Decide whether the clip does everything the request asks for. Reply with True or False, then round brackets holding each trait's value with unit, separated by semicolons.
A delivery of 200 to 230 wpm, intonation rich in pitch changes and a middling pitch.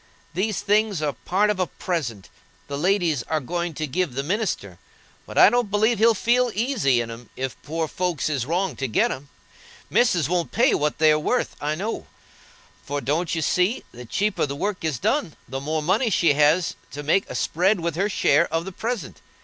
True (205 wpm; 5.8 semitones; 170 Hz)